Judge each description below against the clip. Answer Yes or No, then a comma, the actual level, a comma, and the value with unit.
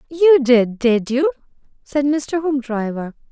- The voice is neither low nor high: No, very high, 270 Hz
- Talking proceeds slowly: Yes, slow, 125 wpm